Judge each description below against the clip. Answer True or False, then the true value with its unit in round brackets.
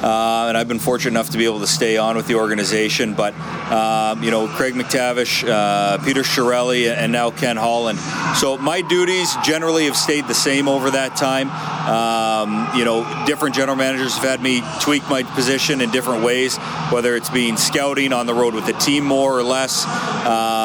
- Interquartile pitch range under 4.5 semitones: True (3.2 semitones)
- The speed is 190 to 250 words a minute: True (200 wpm)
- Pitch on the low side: True (125 Hz)